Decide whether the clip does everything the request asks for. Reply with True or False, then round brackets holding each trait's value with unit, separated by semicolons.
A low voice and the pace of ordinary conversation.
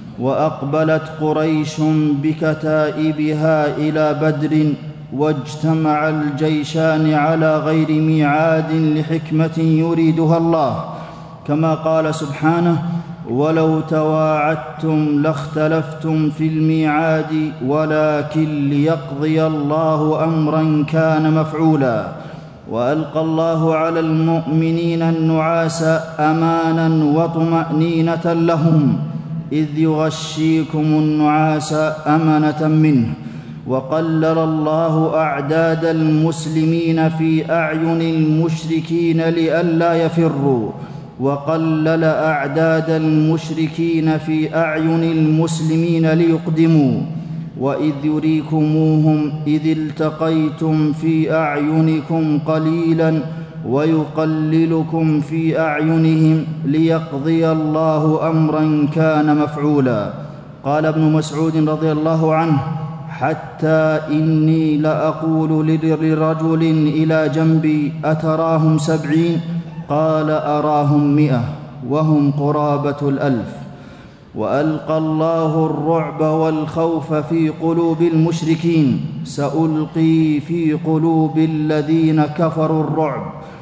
False (155 Hz; 75 wpm)